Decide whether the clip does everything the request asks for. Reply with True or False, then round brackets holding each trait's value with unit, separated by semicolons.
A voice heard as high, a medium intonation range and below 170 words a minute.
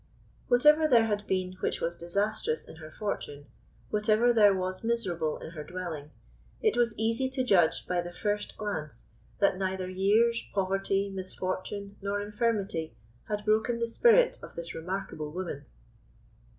True (200 Hz; 3.8 semitones; 150 wpm)